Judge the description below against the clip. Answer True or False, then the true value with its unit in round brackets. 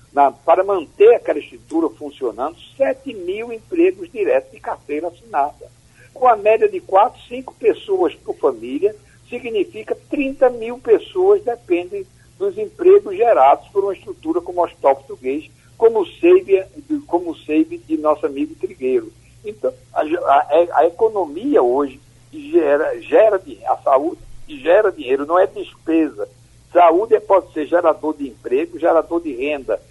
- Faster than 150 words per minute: False (140 wpm)